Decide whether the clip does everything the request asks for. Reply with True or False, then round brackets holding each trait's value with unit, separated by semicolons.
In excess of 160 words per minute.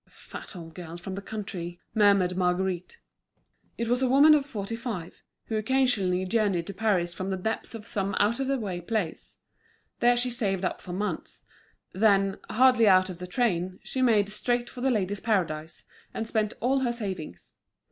True (185 wpm)